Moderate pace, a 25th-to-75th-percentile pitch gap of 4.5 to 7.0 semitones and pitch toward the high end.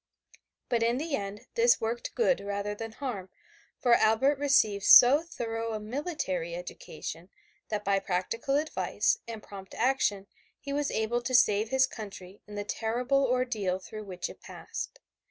Yes: average, 155 wpm; average, 4.8 semitones; high, 225 Hz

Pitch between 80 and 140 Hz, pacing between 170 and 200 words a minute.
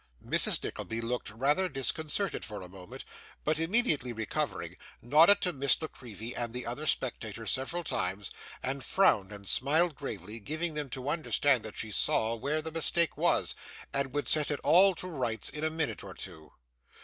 Yes: low, 135 Hz; average, 175 wpm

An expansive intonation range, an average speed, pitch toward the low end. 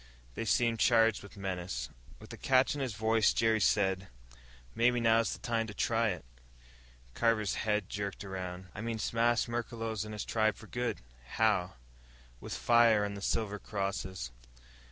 No: average, 2.7 semitones; average, 160 wpm; low, 110 Hz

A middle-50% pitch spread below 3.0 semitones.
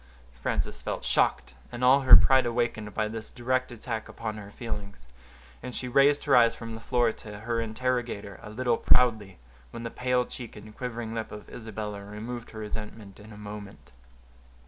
Yes: narrow, 2.6 semitones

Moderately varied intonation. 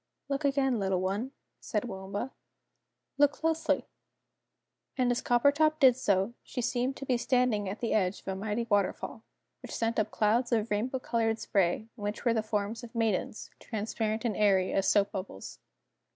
Yes: average, 3.4 semitones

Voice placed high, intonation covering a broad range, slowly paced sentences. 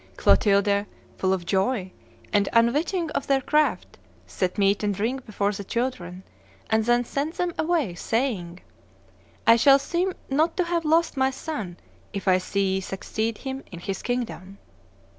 No: high, 230 Hz; wide, 6.1 semitones; average, 160 wpm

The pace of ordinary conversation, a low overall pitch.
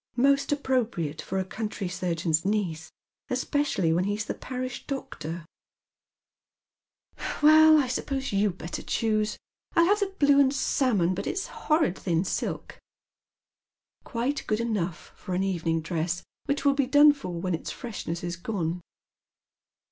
No: average, 155 wpm; high, 210 Hz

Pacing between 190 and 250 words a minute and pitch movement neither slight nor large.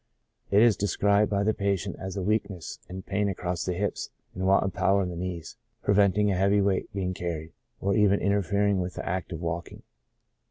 No: average, 200 wpm; narrow, 2.0 semitones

